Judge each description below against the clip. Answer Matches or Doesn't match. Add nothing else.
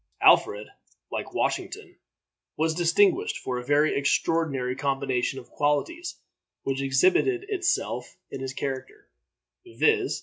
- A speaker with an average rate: Doesn't match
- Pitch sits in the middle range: Matches